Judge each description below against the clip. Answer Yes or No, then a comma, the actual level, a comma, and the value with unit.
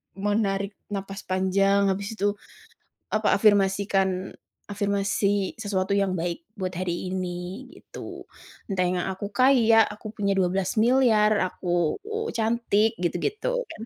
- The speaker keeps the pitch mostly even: Yes, narrow, 2.3 semitones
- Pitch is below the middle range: No, high, 200 Hz